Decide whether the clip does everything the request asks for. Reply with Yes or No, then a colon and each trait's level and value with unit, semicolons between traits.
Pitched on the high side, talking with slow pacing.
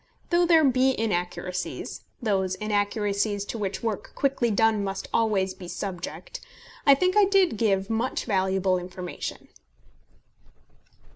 Yes: high, 210 Hz; slow, 125 wpm